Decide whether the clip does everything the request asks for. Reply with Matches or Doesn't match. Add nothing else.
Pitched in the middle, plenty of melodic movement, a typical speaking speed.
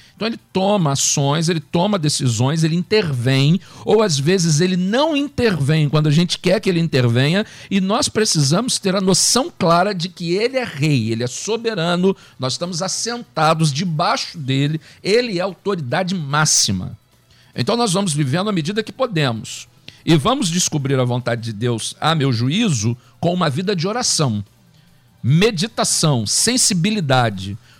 Matches